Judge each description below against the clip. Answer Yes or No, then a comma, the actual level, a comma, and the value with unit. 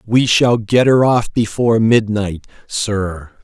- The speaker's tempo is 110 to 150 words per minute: Yes, average, 140 wpm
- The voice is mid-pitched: No, low, 110 Hz